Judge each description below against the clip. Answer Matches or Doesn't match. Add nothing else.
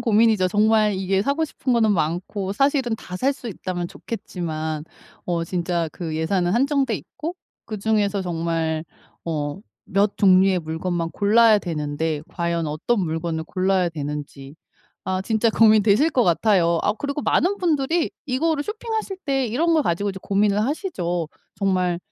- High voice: Matches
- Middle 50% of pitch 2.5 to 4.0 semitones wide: Doesn't match